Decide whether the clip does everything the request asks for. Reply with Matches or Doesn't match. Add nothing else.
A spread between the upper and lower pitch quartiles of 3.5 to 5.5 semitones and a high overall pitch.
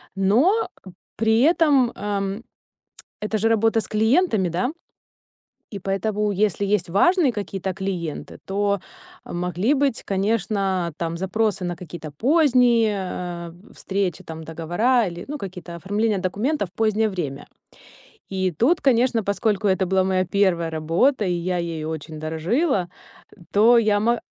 Matches